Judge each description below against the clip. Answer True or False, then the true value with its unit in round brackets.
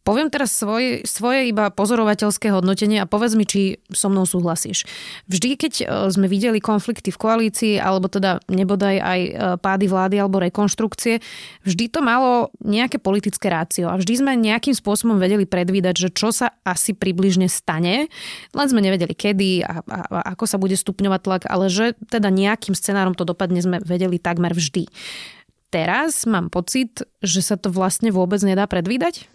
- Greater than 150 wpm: True (165 wpm)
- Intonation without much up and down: False (3.1 semitones)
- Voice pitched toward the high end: True (200 Hz)